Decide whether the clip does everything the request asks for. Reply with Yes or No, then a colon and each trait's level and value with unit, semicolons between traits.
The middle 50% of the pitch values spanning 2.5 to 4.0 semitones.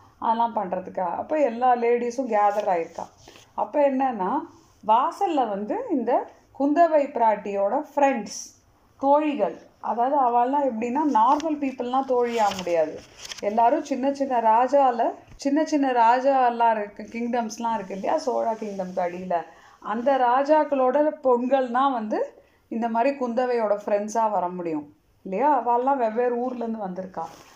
No: average, 4.8 semitones